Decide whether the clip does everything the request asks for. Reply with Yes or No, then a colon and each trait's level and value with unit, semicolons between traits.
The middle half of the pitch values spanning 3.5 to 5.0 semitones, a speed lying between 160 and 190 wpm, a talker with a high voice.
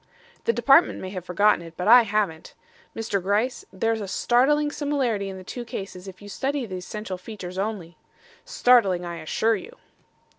Yes: average, 4.6 semitones; average, 175 wpm; high, 205 Hz